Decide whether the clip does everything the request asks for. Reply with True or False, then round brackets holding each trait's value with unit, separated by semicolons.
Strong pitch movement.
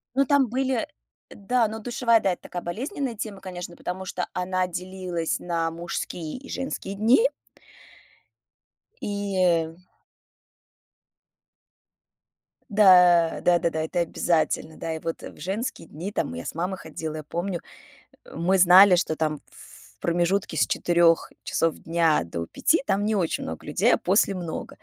False (3.5 semitones)